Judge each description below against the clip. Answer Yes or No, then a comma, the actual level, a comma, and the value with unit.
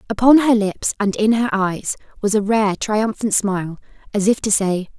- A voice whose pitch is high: Yes, high, 210 Hz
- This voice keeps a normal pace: Yes, average, 195 wpm